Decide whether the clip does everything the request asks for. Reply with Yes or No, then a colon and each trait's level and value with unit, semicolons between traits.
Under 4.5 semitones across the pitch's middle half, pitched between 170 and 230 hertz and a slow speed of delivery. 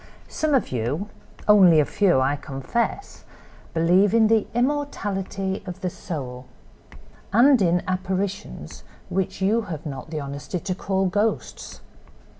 No: average, 5.0 semitones; high, 190 Hz; slow, 120 wpm